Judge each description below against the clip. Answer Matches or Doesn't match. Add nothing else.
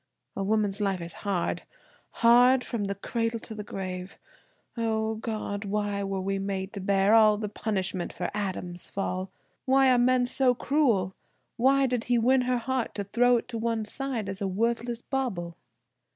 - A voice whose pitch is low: Doesn't match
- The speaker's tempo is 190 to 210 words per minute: Doesn't match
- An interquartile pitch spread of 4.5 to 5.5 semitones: Doesn't match